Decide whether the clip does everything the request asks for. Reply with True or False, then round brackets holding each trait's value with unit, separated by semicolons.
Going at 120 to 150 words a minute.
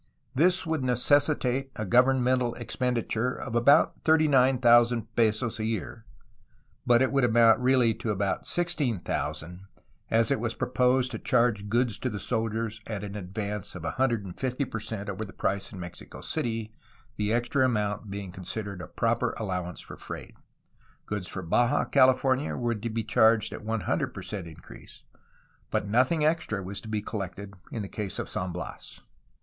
False (165 wpm)